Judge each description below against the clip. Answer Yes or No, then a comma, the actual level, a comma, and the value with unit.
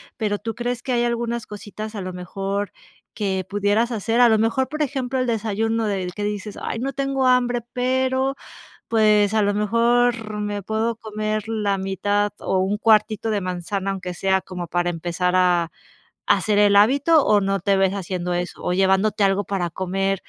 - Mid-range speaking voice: No, high, 210 Hz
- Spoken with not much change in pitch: No, average, 3.2 semitones